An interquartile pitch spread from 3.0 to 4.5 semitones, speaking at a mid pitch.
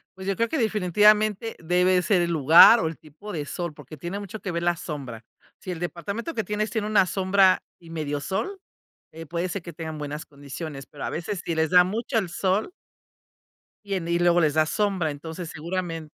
Yes: average, 3.9 semitones; medium, 175 Hz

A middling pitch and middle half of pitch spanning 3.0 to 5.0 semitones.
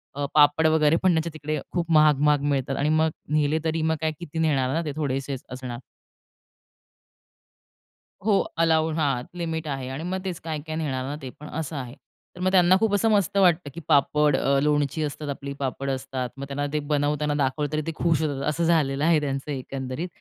No: medium, 150 Hz; narrow, 2.6 semitones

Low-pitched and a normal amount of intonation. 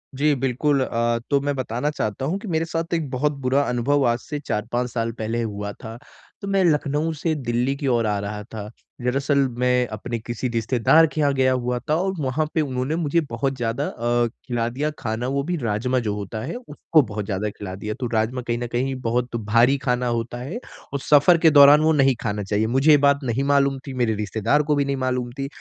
Yes: low, 125 Hz; average, 3.5 semitones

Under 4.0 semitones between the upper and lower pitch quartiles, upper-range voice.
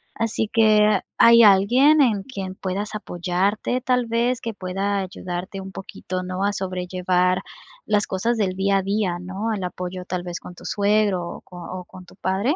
Yes: average, 2.8 semitones; high, 195 Hz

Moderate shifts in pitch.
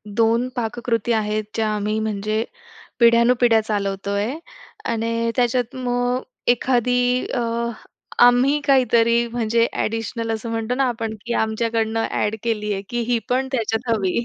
No: narrow, 1.9 semitones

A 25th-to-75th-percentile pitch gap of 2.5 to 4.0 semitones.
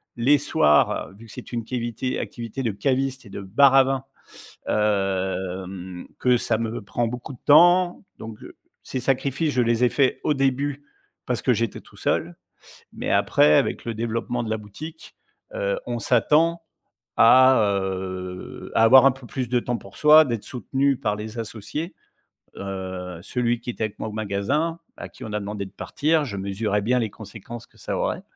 No: average, 4.6 semitones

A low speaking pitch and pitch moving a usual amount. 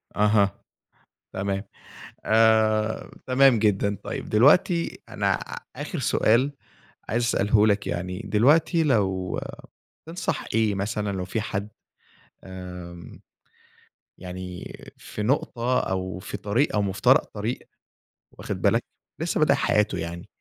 Yes: low, 105 Hz; average, 3.5 semitones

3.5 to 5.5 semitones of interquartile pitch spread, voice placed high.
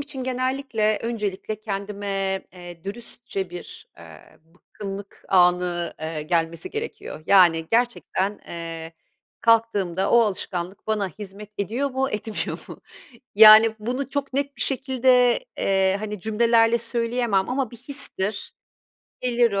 Yes: average, 4.1 semitones; high, 210 Hz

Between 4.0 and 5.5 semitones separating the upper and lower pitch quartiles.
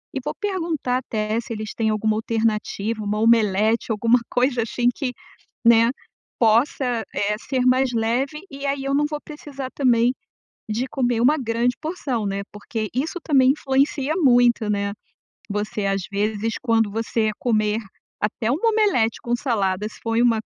No: average, 3.5 semitones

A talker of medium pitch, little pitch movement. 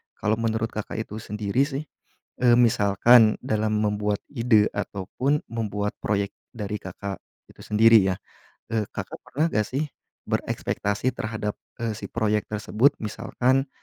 No: low, 110 Hz; narrow, 2.3 semitones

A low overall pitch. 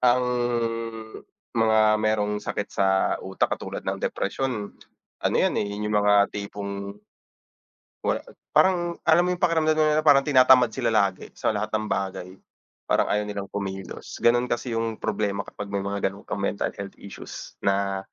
Yes: low, 105 Hz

